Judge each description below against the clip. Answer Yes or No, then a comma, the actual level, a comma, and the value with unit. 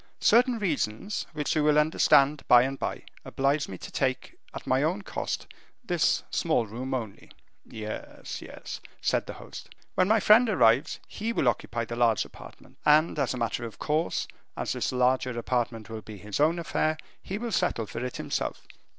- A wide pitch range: Yes, wide, 5.7 semitones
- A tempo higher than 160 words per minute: Yes, average, 180 wpm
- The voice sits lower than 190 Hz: Yes, low, 135 Hz